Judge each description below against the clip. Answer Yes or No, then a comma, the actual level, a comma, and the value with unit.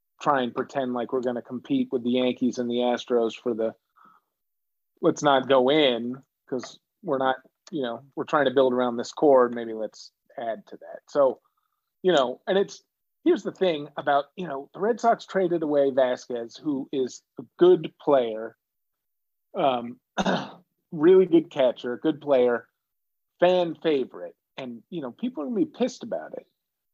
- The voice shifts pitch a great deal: Yes, wide, 6.9 semitones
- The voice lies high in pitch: No, medium, 140 Hz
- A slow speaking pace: No, average, 175 wpm